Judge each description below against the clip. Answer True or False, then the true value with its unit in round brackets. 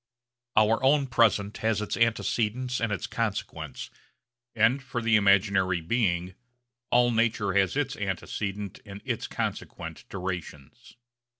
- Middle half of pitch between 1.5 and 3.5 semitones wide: True (3.2 semitones)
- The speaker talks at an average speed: False (120 wpm)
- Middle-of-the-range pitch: False (105 Hz)